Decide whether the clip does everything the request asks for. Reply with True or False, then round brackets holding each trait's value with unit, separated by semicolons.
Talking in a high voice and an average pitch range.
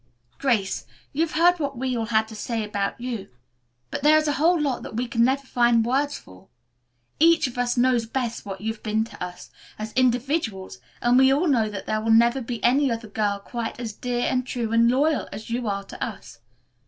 True (240 Hz; 3.4 semitones)